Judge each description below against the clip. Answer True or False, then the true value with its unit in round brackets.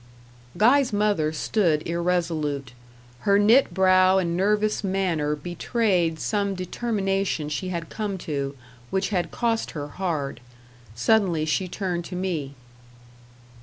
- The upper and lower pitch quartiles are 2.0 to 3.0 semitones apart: False (4.1 semitones)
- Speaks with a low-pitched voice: False (185 Hz)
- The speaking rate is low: True (120 wpm)